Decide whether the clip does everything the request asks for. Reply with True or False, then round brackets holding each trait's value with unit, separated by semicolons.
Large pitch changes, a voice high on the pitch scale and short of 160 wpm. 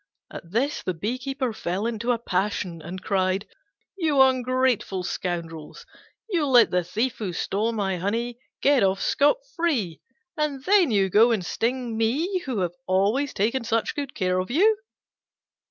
True (5.9 semitones; 225 Hz; 150 wpm)